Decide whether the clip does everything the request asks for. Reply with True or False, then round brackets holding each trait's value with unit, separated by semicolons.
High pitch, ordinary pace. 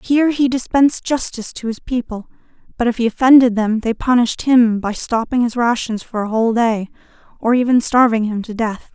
True (235 Hz; 195 wpm)